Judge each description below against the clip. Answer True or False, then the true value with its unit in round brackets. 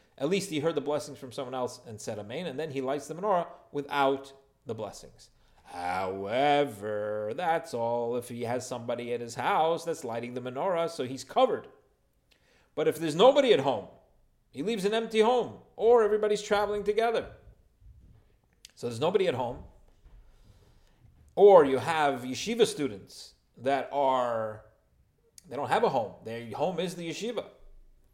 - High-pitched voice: False (140 Hz)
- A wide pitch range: True (7.9 semitones)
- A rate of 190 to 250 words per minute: False (160 wpm)